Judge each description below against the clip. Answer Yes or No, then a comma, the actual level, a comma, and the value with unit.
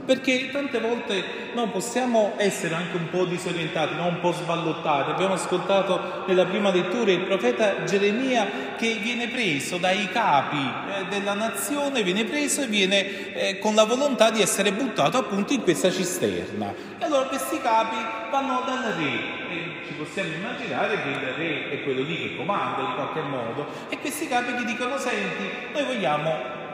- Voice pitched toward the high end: Yes, high, 200 Hz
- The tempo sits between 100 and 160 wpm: No, fast, 170 wpm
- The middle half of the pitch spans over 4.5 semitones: Yes, average, 5.2 semitones